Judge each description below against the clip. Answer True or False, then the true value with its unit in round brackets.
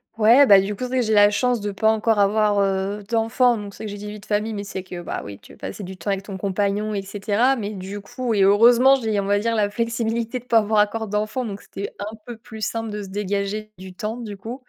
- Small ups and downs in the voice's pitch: True (2.1 semitones)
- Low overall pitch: False (210 Hz)